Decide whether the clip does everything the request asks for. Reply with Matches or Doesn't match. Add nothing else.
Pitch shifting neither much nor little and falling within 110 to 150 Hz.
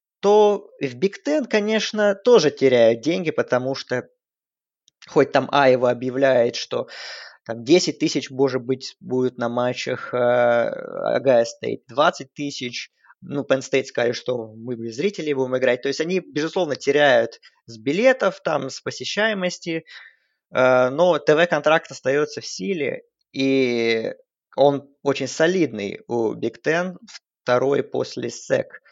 Doesn't match